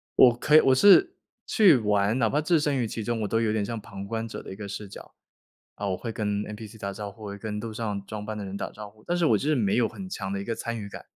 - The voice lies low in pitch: Yes, low, 110 Hz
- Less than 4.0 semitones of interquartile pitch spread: Yes, average, 2.7 semitones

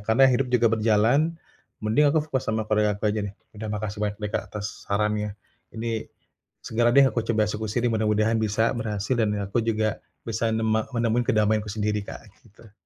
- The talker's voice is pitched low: Yes, low, 110 Hz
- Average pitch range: No, narrow, 1.6 semitones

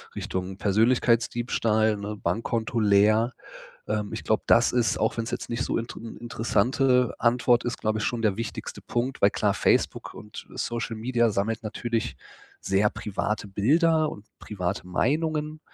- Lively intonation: No, narrow, 2.4 semitones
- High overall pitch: No, low, 115 Hz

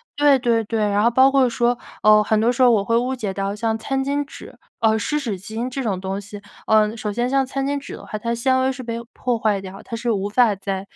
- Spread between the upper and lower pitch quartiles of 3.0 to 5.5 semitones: Yes, average, 3.6 semitones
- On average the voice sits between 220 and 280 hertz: Yes, high, 230 Hz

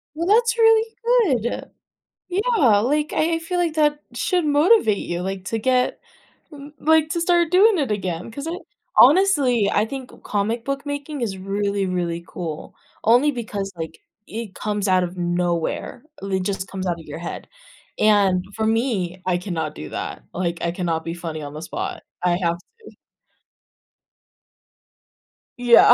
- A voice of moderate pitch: No, high, 215 Hz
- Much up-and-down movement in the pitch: Yes, wide, 8.7 semitones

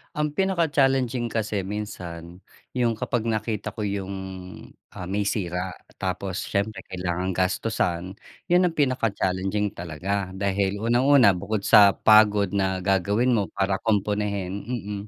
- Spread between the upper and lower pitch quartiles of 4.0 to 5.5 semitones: No, average, 3.2 semitones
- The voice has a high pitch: No, low, 100 Hz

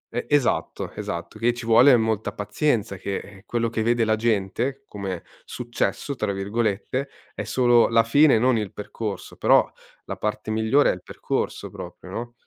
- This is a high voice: No, low, 115 Hz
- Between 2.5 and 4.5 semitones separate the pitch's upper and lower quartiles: Yes, average, 2.8 semitones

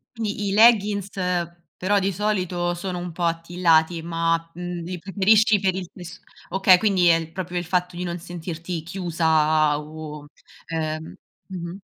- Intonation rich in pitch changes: No, narrow, 2.5 semitones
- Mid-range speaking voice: Yes, medium, 175 Hz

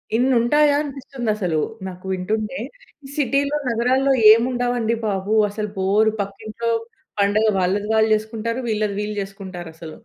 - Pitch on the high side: Yes, high, 220 Hz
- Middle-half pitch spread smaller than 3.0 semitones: No, average, 3.6 semitones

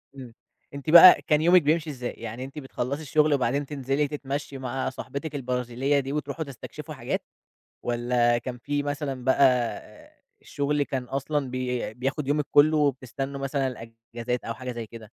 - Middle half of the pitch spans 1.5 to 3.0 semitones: Yes, average, 2.7 semitones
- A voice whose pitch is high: No, low, 135 Hz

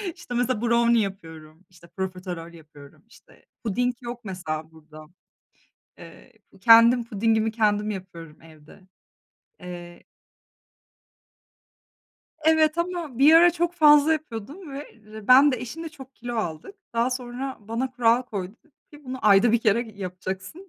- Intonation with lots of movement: Yes, wide, 5.9 semitones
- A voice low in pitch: No, high, 230 Hz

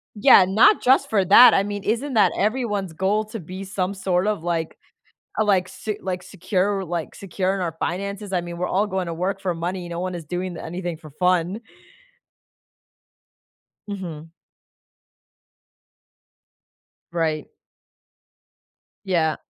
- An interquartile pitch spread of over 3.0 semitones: No, narrow, 2.6 semitones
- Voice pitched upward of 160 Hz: Yes, medium, 185 Hz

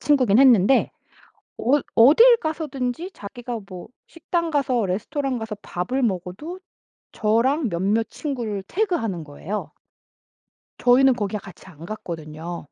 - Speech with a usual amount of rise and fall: No, wide, 6.5 semitones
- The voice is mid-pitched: No, high, 235 Hz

